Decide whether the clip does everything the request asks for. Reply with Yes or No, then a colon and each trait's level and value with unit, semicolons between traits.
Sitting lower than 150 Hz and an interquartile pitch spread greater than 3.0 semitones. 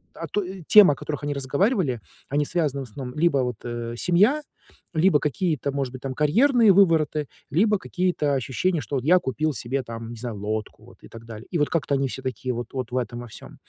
Yes: medium, 140 Hz; wide, 5.6 semitones